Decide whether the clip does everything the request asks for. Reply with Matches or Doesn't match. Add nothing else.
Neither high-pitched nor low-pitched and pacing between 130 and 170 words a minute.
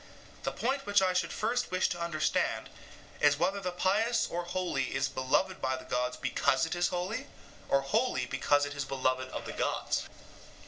Doesn't match